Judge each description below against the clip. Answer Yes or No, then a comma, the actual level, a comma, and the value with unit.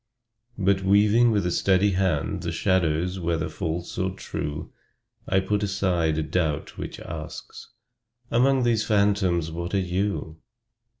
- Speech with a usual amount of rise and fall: Yes, average, 3.4 semitones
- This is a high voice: No, very low, 95 Hz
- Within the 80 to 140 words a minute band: Yes, slow, 135 wpm